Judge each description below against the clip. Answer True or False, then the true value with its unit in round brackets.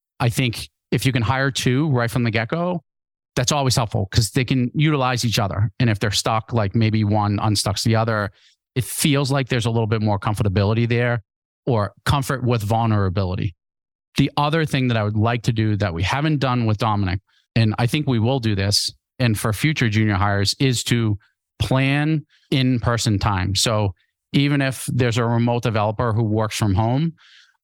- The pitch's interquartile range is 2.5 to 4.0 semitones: True (3.7 semitones)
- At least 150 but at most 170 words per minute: False (195 wpm)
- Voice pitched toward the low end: True (120 Hz)